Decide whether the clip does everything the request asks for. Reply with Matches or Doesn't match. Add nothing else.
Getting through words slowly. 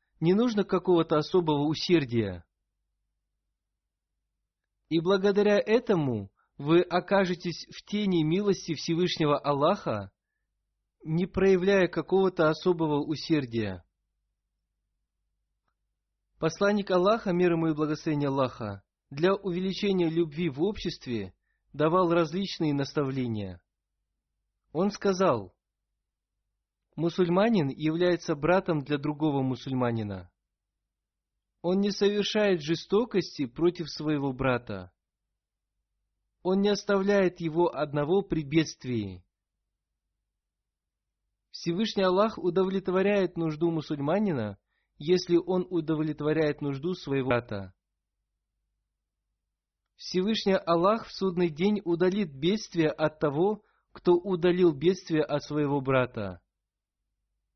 Matches